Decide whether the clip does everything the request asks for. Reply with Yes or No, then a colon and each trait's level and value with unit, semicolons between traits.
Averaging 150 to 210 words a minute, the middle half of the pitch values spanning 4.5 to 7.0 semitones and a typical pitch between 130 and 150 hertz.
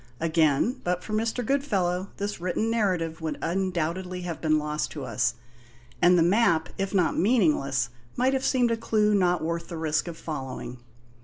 No: average, 170 wpm; average, 4.8 semitones; medium, 175 Hz